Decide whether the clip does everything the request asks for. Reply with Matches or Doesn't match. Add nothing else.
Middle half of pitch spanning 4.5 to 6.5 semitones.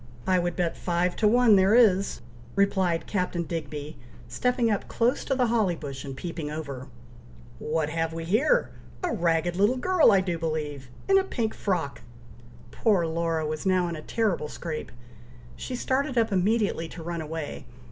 Matches